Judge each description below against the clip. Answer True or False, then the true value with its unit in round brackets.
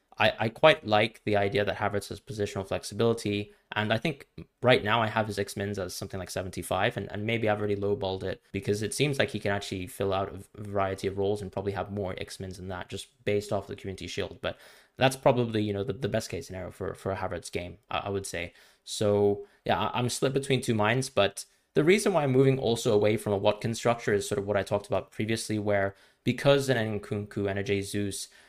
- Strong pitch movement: False (2.6 semitones)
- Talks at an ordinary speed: False (230 wpm)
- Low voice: True (105 Hz)